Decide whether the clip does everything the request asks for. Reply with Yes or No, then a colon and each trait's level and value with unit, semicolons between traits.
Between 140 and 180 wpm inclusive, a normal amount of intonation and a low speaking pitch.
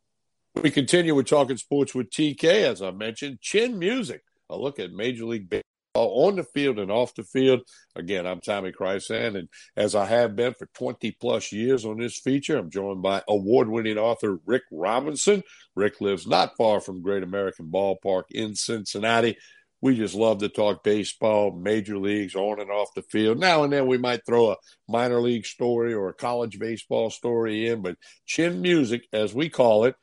No: average, 190 wpm; average, 3.9 semitones; low, 115 Hz